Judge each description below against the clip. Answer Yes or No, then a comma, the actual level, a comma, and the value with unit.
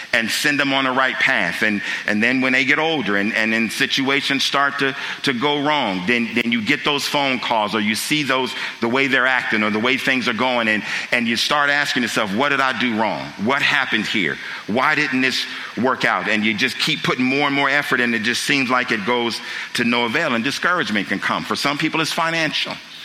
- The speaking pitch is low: Yes, low, 130 Hz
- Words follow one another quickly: Yes, fast, 235 wpm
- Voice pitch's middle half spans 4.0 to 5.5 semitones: No, average, 3.6 semitones